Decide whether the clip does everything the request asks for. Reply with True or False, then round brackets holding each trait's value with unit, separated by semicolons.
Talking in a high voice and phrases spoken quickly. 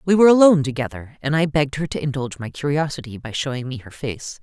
False (140 Hz; 230 wpm)